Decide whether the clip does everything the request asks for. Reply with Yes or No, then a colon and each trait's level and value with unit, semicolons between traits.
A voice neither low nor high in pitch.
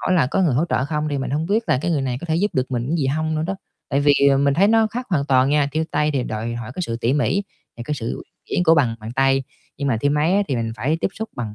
Yes: medium, 145 Hz